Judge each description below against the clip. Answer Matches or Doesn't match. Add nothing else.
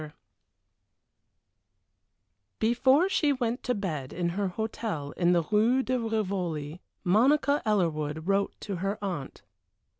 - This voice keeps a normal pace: Doesn't match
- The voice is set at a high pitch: Matches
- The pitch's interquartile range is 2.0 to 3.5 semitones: Doesn't match